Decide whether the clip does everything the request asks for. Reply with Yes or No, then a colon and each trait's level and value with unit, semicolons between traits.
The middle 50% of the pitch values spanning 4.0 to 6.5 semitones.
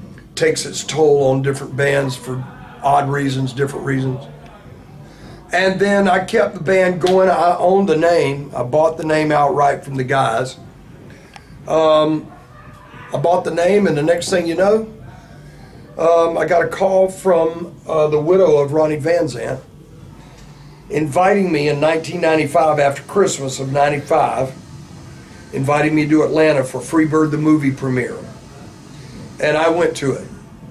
No: average, 3.4 semitones